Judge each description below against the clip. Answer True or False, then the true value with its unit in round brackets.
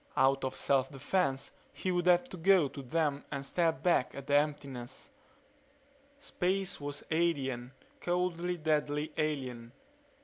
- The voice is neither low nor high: True (150 Hz)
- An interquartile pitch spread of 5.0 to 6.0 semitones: False (4.3 semitones)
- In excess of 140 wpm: False (135 wpm)